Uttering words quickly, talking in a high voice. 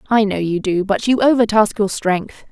Yes: fast, 215 wpm; high, 210 Hz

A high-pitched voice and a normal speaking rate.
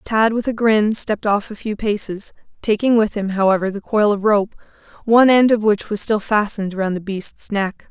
No: high, 210 Hz; fast, 210 wpm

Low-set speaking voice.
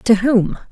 No: high, 220 Hz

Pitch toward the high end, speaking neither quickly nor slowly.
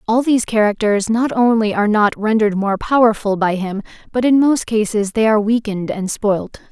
Yes: high, 215 Hz; average, 190 wpm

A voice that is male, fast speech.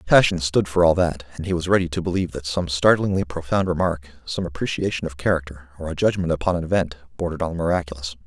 Yes: male; fast, 220 wpm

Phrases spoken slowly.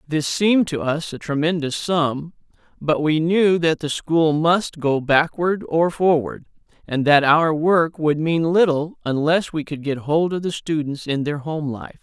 No: average, 185 wpm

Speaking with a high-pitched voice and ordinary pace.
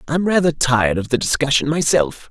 No: medium, 140 Hz; average, 180 wpm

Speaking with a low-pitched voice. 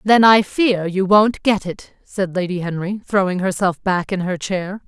No: high, 190 Hz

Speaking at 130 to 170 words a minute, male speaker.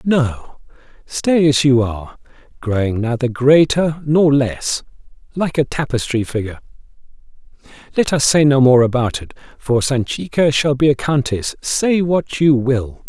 Yes: average, 140 wpm; male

